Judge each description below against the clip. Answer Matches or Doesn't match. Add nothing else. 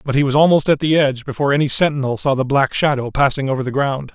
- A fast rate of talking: Matches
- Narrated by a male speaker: Matches